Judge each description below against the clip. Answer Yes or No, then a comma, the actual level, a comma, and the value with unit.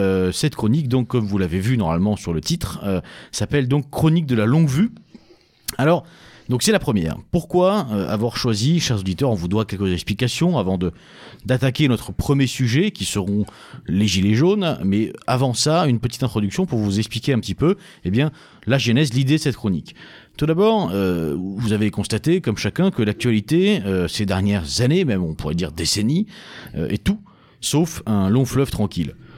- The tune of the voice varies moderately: No, wide, 7.4 semitones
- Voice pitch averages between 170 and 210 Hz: No, low, 120 Hz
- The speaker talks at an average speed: Yes, average, 190 wpm